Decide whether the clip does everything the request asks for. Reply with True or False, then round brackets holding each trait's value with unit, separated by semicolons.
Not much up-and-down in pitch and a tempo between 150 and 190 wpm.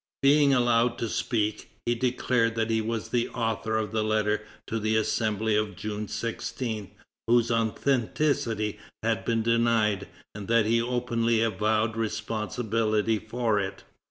False (1.5 semitones; 140 wpm)